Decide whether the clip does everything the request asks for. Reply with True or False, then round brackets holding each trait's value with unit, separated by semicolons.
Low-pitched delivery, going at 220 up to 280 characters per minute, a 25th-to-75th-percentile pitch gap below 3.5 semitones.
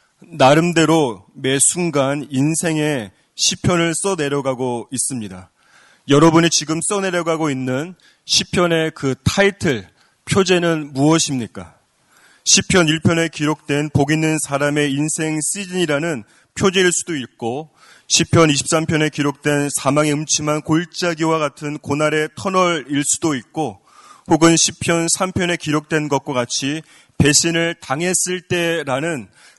False (155 Hz; 260 characters per minute; 2.7 semitones)